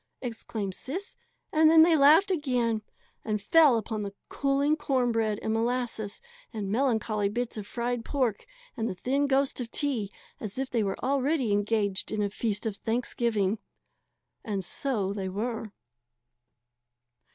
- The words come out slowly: No, average, 150 wpm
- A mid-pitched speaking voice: No, high, 230 Hz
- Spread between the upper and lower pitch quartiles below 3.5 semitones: No, average, 4.5 semitones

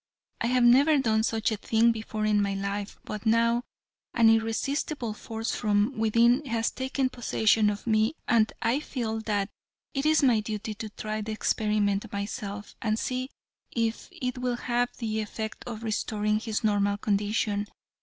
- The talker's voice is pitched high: Yes, high, 220 Hz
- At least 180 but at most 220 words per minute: No, average, 165 wpm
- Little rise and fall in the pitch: Yes, narrow, 2.1 semitones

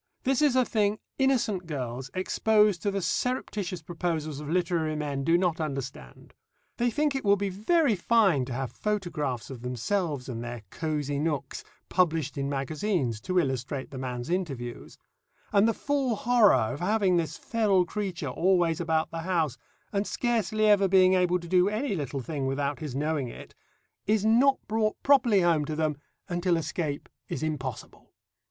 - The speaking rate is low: No, average, 165 wpm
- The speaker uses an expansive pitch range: Yes, wide, 6.3 semitones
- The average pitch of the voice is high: No, medium, 175 Hz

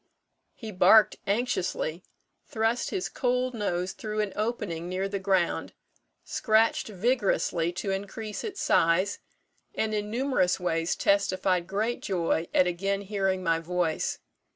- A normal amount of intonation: Yes, average, 3.4 semitones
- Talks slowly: Yes, slow, 130 wpm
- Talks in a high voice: Yes, high, 195 Hz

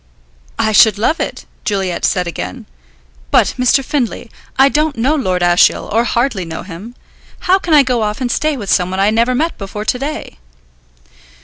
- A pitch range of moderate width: No, wide, 6.0 semitones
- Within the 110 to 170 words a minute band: No, average, 180 wpm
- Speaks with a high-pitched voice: Yes, high, 230 Hz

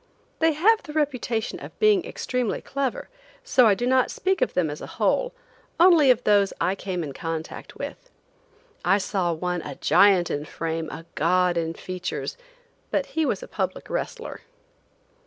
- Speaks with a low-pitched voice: No, high, 205 Hz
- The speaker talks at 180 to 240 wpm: No, average, 170 wpm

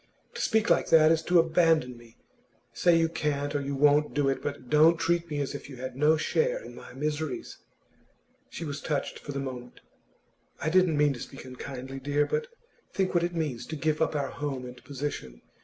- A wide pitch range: No, average, 3.2 semitones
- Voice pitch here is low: No, medium, 150 Hz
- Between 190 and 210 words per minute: Yes, fast, 205 wpm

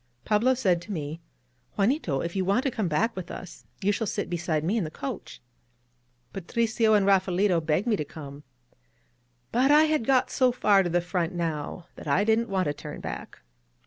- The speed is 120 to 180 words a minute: No, average, 195 wpm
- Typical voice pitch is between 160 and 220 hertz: Yes, high, 190 Hz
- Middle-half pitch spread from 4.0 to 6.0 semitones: Yes, average, 5.0 semitones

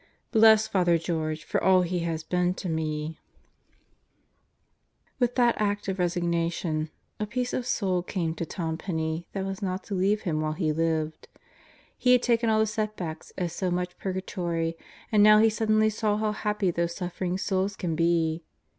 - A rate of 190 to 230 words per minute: No, average, 170 wpm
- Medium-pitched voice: Yes, medium, 180 Hz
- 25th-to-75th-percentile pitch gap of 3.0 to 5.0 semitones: Yes, average, 4.2 semitones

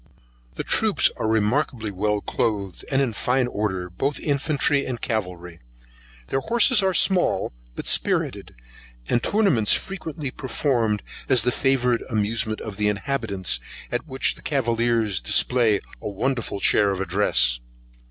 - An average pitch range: Yes, average, 4.7 semitones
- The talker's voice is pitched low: Yes, low, 115 Hz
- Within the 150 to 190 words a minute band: No, slow, 135 wpm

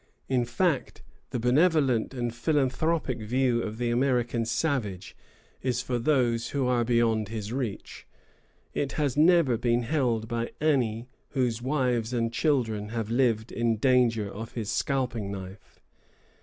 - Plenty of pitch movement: No, average, 2.7 semitones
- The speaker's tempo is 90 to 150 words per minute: Yes, average, 140 wpm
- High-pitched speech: No, low, 120 Hz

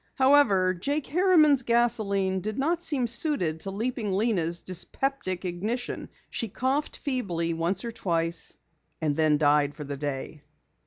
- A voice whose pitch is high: Yes, high, 200 Hz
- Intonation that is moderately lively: No, wide, 7.6 semitones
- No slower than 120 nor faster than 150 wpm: Yes, average, 140 wpm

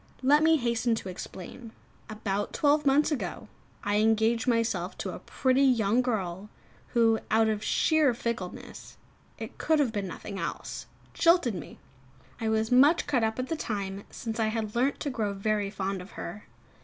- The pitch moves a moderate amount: Yes, average, 3.8 semitones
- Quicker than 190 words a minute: No, average, 170 wpm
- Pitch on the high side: Yes, high, 225 Hz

